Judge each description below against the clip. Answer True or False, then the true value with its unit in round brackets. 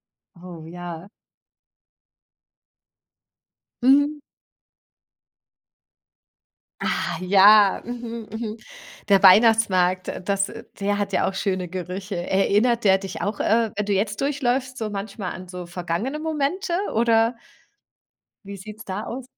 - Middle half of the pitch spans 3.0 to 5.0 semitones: True (3.8 semitones)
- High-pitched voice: True (205 Hz)